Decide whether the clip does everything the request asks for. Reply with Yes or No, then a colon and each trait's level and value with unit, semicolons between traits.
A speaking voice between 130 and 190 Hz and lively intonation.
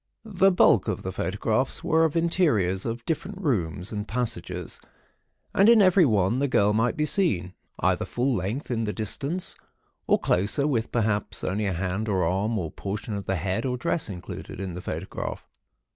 No: low, 110 Hz; wide, 7.3 semitones